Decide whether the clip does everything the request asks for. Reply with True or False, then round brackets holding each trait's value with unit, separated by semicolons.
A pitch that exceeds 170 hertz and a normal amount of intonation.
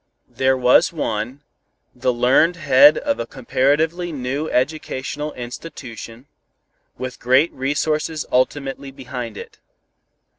False (135 Hz; 3.3 semitones)